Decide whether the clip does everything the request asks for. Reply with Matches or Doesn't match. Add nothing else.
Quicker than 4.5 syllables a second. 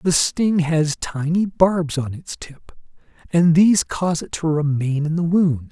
Doesn't match